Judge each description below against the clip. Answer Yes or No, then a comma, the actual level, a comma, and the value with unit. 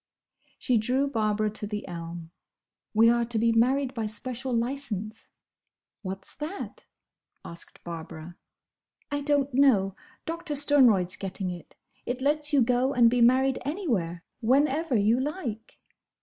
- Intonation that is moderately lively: Yes, average, 4.9 semitones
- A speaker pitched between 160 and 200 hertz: No, high, 240 Hz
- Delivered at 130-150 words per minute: Yes, slow, 135 wpm